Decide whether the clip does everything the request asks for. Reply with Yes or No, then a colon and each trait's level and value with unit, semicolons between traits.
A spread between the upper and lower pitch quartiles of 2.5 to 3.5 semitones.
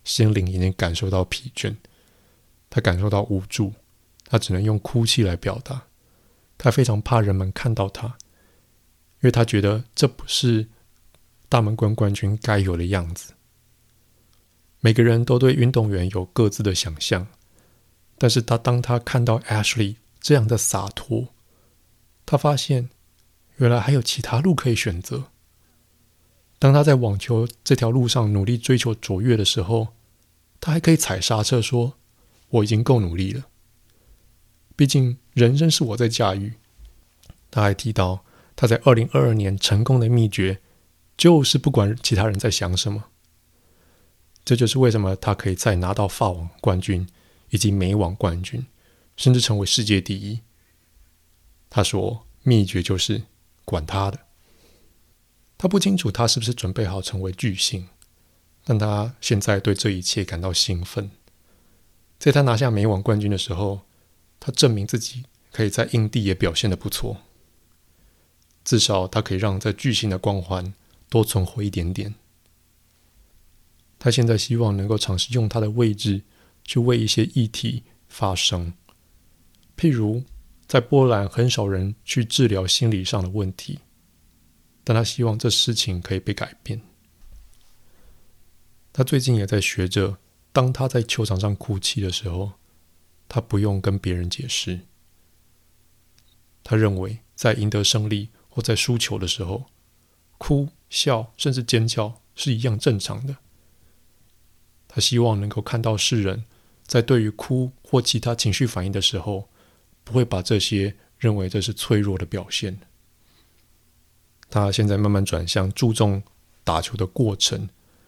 No: average, 4.3 semitones